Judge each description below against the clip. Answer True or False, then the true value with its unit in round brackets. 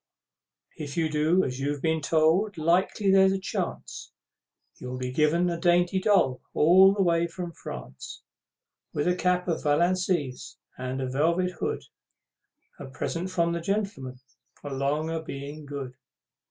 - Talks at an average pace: True (145 wpm)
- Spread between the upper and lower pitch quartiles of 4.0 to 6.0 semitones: True (4.3 semitones)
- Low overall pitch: False (165 Hz)